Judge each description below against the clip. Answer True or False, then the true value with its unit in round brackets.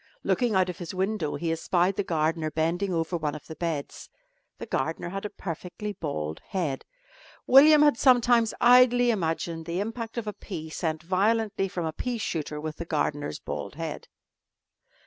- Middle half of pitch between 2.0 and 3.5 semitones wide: False (5.3 semitones)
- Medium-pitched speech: True (180 Hz)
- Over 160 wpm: True (170 wpm)